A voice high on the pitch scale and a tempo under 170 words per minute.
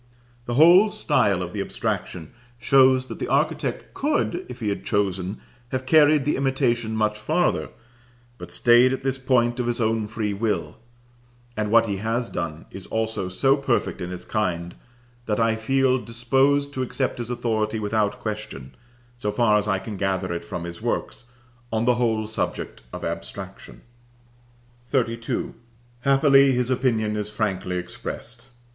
No: low, 115 Hz; average, 160 wpm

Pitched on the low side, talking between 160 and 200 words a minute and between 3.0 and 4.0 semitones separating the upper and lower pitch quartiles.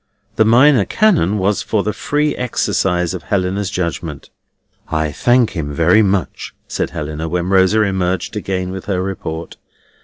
No: very low, 95 Hz; average, 150 wpm; average, 3.6 semitones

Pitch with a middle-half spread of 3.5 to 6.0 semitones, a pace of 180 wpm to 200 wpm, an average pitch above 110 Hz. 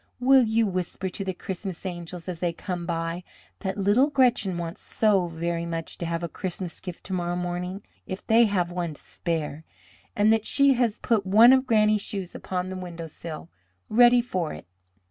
Yes: average, 3.8 semitones; average, 185 wpm; medium, 185 Hz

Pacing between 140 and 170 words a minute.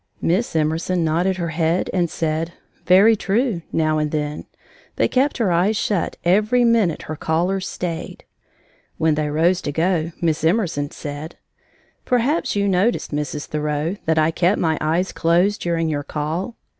Yes: average, 155 wpm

